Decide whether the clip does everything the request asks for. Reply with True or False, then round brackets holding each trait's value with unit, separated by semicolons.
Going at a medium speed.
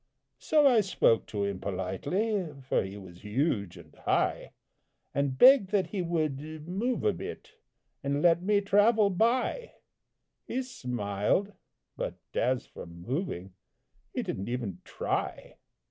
False (130 wpm)